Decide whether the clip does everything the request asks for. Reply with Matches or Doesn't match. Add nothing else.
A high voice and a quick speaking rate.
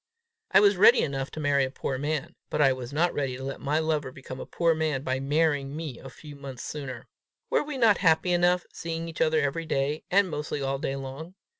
Doesn't match